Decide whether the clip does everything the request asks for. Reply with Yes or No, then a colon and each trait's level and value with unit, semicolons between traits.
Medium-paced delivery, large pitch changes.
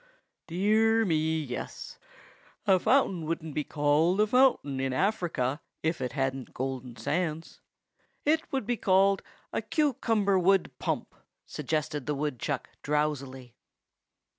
No: slow, 120 wpm; wide, 6.1 semitones